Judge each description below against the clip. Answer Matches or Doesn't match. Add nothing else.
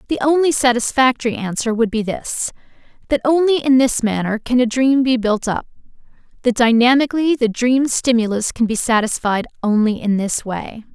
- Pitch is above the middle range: Matches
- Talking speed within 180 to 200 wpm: Doesn't match